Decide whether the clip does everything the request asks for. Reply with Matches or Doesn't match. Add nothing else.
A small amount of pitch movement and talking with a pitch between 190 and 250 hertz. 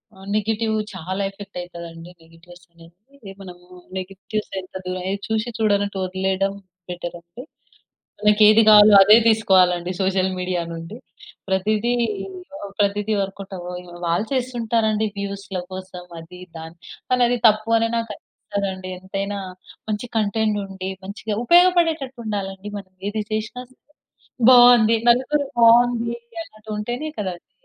Doesn't match